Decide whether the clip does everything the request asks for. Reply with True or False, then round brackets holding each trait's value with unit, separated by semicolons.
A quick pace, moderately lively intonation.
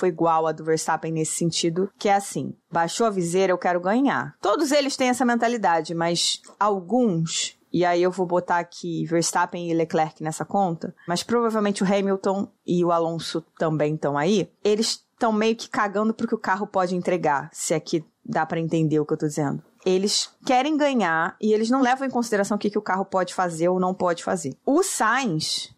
True (205 wpm; 4.4 semitones)